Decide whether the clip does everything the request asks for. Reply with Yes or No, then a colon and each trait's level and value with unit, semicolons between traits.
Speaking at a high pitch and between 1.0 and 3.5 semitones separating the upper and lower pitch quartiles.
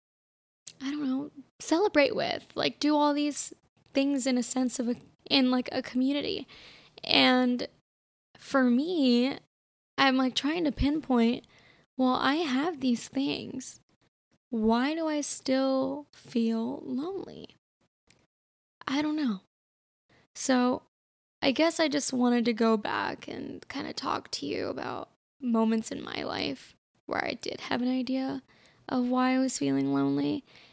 Yes: very high, 260 Hz; narrow, 2.5 semitones